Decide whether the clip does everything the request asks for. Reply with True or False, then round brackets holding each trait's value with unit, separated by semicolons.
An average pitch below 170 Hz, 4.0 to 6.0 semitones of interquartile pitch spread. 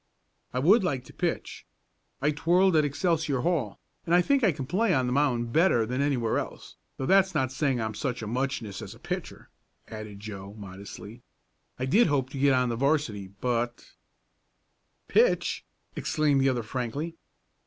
True (135 Hz; 5.0 semitones)